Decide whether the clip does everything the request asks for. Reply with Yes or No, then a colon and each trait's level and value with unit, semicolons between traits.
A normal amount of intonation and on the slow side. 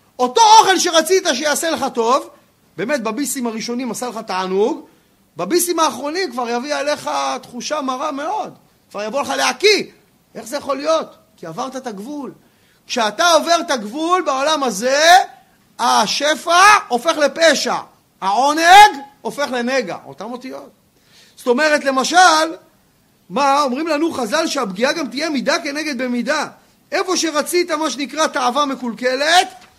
No: average, 4.3 semitones; average, 130 wpm